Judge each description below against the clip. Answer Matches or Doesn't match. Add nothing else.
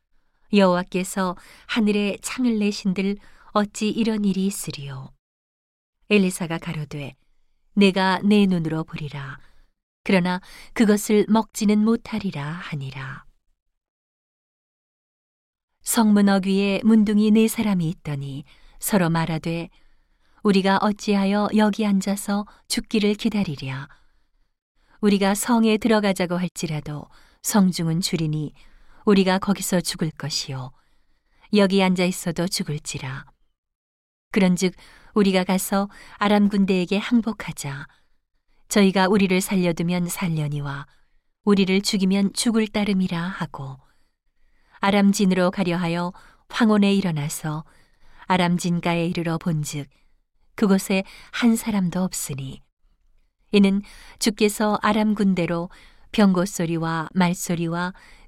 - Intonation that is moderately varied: Matches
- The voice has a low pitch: Doesn't match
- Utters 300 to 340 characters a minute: Doesn't match